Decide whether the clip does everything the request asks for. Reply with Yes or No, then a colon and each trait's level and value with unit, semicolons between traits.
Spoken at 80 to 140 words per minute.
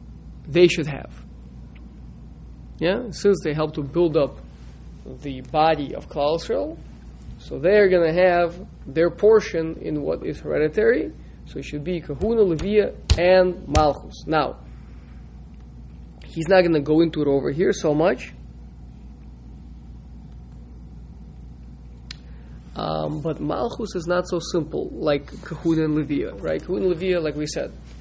Yes: slow, 135 wpm